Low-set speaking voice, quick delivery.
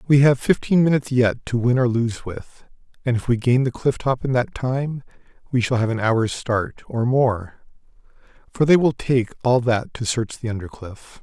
Yes: low, 125 Hz; fast, 210 wpm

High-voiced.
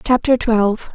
Yes: high, 230 Hz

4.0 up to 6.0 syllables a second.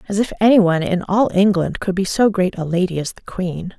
Yes: 5.7 syllables/s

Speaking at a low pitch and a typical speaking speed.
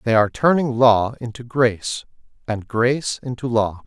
Yes: low, 120 Hz; average, 155 wpm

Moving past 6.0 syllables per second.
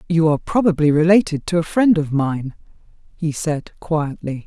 No: 5.0 syllables/s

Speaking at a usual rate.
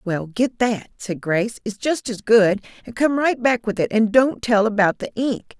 No: fast, 225 wpm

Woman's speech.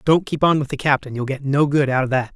No: male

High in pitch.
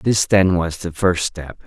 No: very low, 90 Hz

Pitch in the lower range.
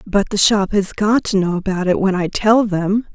No: high, 200 Hz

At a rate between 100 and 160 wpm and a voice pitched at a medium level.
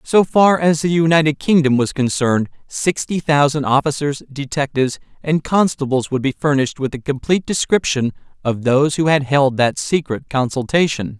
Yes: average, 155 wpm; medium, 145 Hz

